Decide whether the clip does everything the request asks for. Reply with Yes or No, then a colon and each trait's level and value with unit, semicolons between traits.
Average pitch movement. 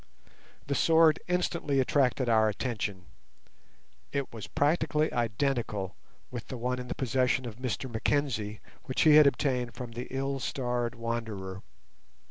Yes: average, 3.4 semitones